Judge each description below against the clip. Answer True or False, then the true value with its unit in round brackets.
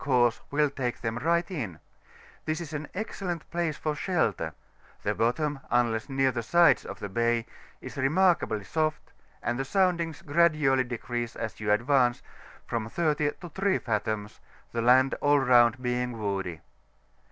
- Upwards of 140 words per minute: True (150 wpm)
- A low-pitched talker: True (130 Hz)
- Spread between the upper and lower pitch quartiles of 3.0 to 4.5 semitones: False (5.0 semitones)